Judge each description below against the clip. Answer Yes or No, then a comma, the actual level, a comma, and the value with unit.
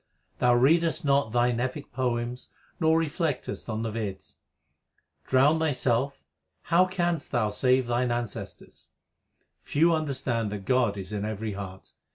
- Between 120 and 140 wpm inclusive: Yes, slow, 135 wpm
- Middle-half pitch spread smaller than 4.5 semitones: No, average, 4.9 semitones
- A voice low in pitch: Yes, low, 125 Hz